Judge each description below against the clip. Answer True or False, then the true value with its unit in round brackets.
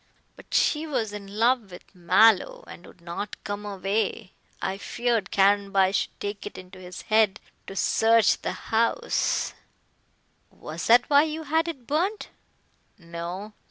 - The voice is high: True (210 Hz)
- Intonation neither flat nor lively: True (4.1 semitones)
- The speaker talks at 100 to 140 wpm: False (150 wpm)